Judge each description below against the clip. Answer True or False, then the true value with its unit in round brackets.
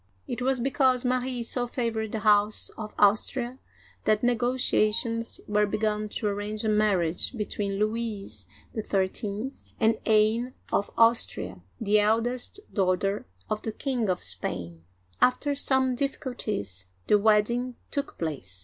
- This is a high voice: True (215 Hz)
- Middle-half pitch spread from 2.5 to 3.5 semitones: True (3.1 semitones)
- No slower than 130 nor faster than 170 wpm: True (135 wpm)